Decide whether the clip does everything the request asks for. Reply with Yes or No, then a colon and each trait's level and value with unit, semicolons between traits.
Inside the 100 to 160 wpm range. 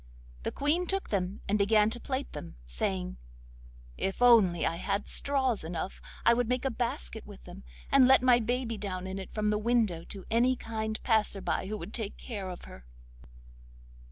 No: average, 185 wpm